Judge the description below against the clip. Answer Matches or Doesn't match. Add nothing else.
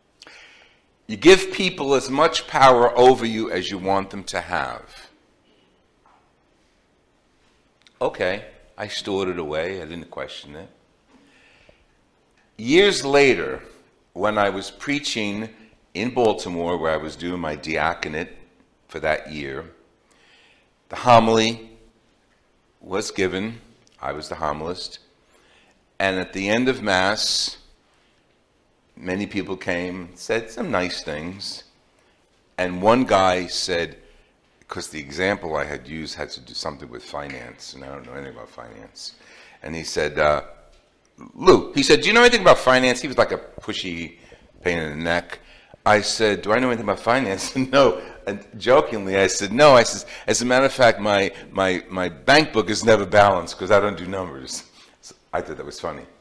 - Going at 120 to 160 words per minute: Matches